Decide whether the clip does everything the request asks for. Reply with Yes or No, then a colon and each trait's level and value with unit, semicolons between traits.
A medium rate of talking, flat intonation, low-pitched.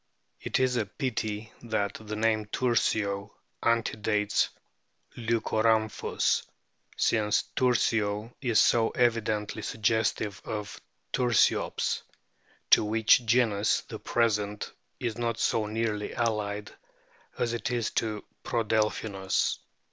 No: slow, 100 wpm; narrow, 1.8 semitones; low, 110 Hz